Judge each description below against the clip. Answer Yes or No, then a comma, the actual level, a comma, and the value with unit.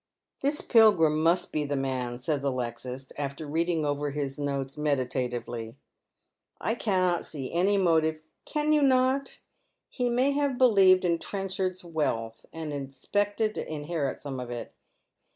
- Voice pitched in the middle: Yes, medium, 155 Hz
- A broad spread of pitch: Yes, wide, 6.5 semitones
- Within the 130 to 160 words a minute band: Yes, average, 155 wpm